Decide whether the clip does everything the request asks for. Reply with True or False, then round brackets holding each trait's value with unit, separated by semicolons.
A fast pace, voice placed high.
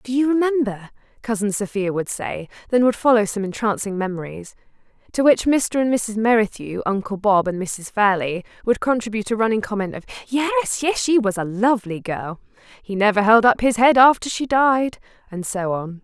False (185 wpm; 220 Hz)